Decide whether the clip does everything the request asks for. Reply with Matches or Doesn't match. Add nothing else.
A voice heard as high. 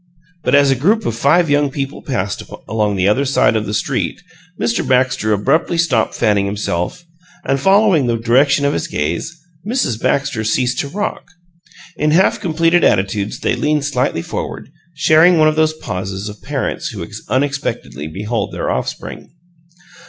Doesn't match